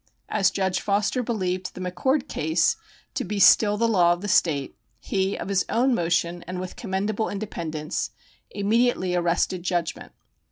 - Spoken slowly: No, average, 155 wpm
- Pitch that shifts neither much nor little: Yes, average, 3.0 semitones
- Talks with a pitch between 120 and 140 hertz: No, high, 190 Hz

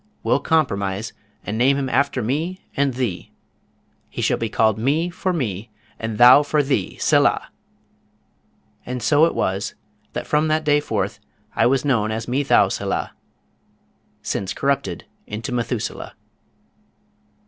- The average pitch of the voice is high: No, low, 130 Hz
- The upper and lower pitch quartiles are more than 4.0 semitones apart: Yes, average, 4.9 semitones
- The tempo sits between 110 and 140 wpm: Yes, slow, 135 wpm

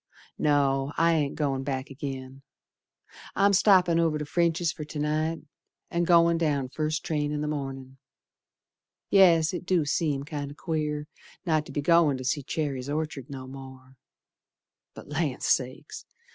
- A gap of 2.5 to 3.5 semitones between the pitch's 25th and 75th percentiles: Yes, average, 3.2 semitones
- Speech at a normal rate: Yes, average, 150 wpm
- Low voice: No, medium, 150 Hz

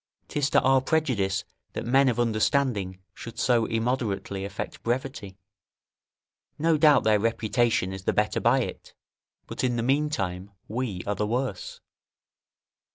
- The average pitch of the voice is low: Yes, low, 115 Hz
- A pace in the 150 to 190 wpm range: No, average, 140 wpm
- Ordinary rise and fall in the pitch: Yes, average, 4.5 semitones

